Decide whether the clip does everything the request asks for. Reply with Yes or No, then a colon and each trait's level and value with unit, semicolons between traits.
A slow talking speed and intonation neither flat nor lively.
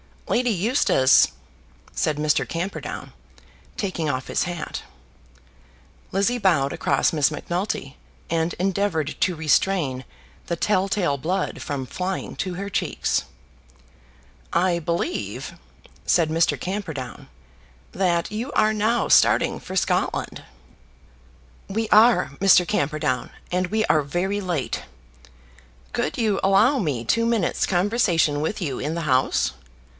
Yes: slow, 120 wpm; average, 4.8 semitones